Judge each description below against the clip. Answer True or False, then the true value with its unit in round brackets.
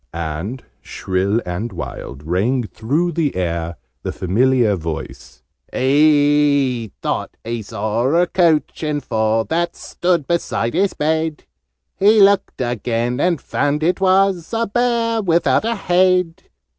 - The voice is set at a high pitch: False (140 Hz)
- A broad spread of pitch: True (7.9 semitones)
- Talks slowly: True (130 wpm)